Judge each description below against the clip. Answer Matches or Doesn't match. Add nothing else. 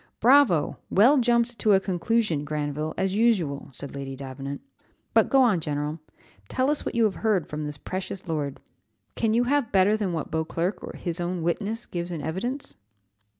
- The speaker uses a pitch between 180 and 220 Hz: Matches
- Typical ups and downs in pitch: Doesn't match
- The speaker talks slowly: Doesn't match